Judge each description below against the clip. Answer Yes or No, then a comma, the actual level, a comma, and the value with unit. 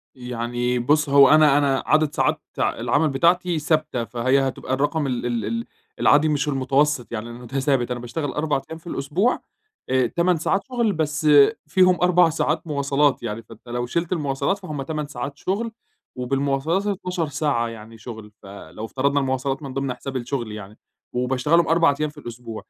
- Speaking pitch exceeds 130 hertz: Yes, medium, 140 Hz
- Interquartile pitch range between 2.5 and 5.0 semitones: Yes, average, 4.2 semitones